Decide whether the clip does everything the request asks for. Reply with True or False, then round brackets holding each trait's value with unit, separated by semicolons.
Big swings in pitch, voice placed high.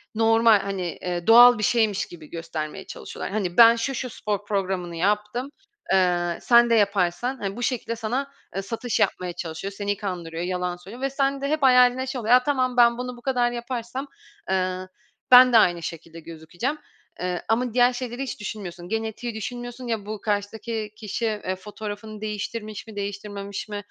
False (4.3 semitones; 215 Hz)